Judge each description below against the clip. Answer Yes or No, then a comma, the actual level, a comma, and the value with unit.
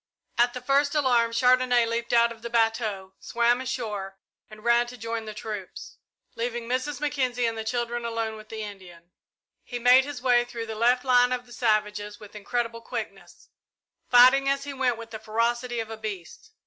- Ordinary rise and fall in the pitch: No, narrow, 2.1 semitones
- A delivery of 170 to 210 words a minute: Yes, average, 185 wpm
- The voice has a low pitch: No, high, 235 Hz